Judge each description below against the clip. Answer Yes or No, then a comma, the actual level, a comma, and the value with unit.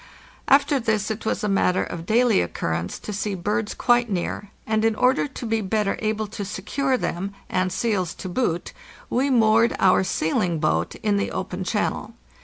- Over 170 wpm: Yes, average, 180 wpm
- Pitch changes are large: No, average, 3.6 semitones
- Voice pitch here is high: Yes, high, 210 Hz